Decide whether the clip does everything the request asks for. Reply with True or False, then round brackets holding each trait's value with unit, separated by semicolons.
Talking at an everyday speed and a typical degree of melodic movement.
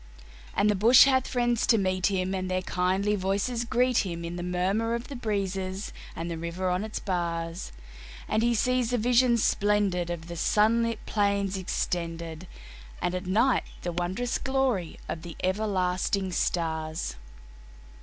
True (155 wpm; 4.3 semitones)